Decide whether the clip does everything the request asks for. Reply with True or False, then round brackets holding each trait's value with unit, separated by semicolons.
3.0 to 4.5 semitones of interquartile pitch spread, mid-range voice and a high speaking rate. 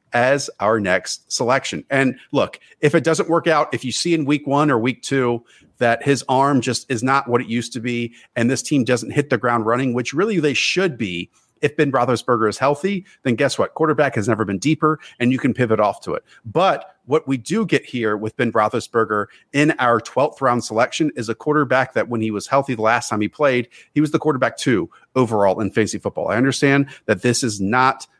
False (3.7 semitones; 125 Hz; 225 wpm)